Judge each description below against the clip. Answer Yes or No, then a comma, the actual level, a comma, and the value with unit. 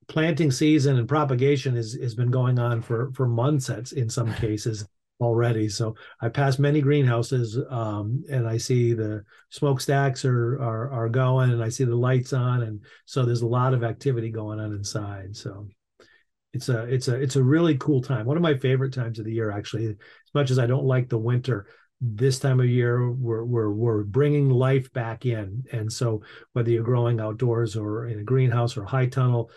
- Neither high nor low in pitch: No, low, 125 Hz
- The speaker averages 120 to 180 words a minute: No, fast, 205 wpm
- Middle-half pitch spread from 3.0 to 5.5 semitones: No, narrow, 2.6 semitones